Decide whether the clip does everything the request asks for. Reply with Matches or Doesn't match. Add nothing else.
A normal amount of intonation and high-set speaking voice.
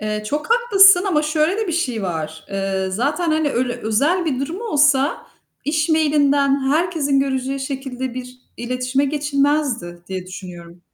Matches